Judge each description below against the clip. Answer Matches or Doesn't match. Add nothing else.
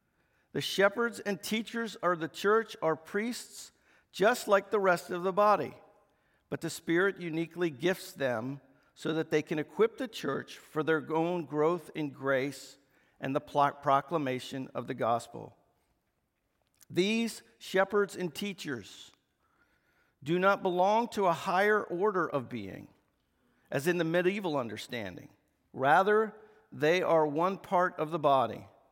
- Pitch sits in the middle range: Matches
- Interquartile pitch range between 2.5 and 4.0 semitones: Doesn't match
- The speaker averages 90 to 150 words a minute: Matches